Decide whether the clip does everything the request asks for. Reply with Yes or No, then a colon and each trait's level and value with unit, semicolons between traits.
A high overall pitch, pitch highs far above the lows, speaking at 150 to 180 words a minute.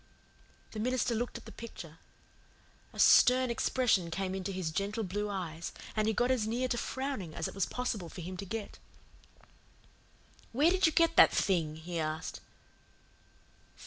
Yes: high, 205 Hz; wide, 5.8 semitones; average, 165 wpm